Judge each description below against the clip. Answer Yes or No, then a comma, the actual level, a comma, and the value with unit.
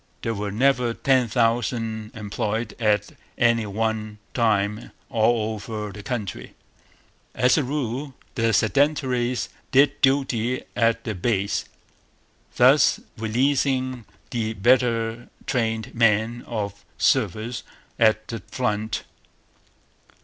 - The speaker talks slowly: Yes, slow, 105 wpm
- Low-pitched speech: Yes, low, 115 Hz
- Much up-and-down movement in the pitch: No, narrow, 2.5 semitones